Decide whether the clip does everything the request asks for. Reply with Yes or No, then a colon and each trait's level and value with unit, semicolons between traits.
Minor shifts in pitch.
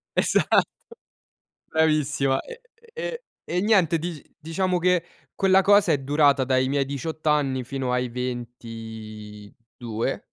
No: average, 4.9 semitones